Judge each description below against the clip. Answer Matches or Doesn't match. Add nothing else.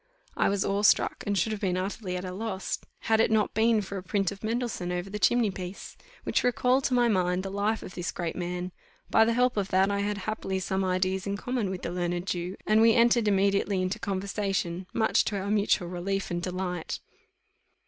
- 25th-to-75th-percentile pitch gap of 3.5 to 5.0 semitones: Doesn't match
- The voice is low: Doesn't match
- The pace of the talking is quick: Matches